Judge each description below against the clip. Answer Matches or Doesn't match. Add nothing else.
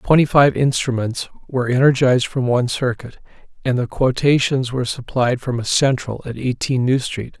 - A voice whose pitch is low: Matches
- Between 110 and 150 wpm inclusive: Doesn't match